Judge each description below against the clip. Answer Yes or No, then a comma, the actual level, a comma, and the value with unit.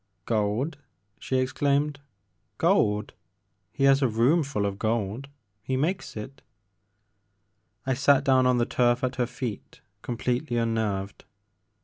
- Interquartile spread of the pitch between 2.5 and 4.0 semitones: No, average, 4.4 semitones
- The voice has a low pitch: Yes, low, 120 Hz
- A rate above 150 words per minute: No, average, 145 wpm